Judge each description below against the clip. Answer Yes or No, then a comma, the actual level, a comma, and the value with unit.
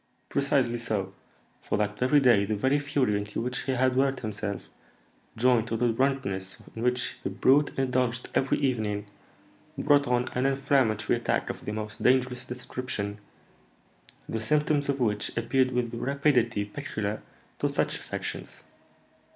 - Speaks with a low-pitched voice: Yes, low, 125 Hz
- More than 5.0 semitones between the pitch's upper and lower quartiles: No, average, 3.8 semitones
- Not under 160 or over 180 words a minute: No, average, 150 wpm